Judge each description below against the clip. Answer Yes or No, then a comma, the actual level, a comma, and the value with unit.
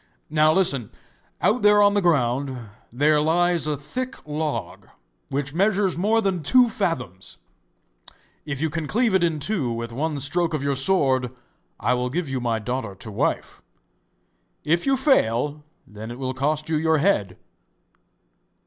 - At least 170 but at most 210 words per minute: No, average, 160 wpm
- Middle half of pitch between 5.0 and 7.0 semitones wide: Yes, wide, 5.5 semitones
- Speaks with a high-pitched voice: No, medium, 150 Hz